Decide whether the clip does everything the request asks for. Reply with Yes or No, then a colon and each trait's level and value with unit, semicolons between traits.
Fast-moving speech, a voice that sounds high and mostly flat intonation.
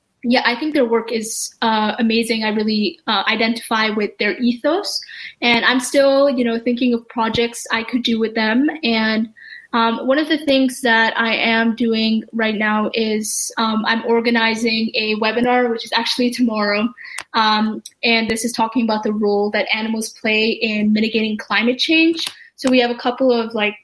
No: average, 180 wpm; high, 230 Hz; narrow, 1.9 semitones